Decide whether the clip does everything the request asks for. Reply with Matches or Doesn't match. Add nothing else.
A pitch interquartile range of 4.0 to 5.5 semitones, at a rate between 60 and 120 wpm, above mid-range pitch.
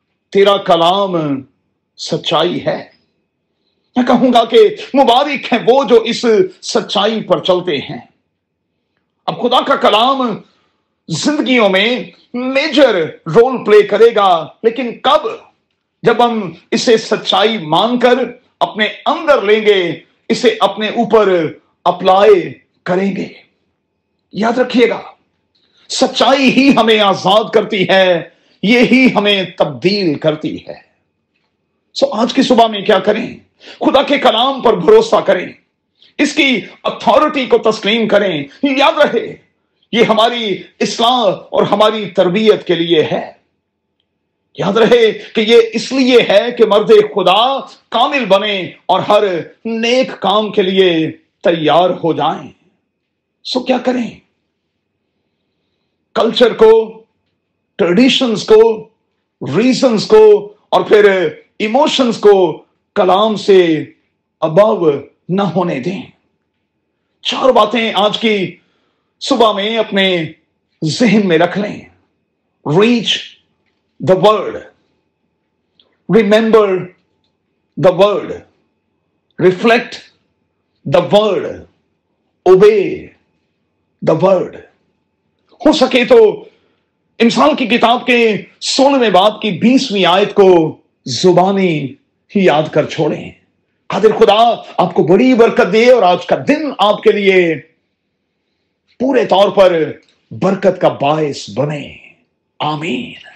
Matches